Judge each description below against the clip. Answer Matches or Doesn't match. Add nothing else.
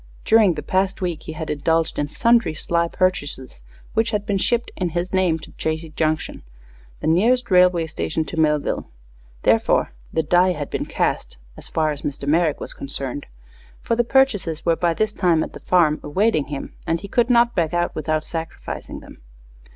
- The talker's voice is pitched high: Doesn't match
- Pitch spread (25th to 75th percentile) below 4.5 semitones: Matches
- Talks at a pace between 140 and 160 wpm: Doesn't match